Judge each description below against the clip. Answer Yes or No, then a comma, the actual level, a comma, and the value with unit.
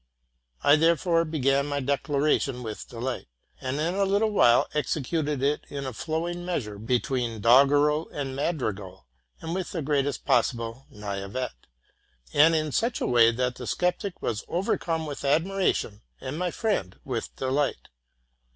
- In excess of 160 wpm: No, average, 140 wpm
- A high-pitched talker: No, medium, 140 Hz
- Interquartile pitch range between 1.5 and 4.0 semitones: No, average, 4.8 semitones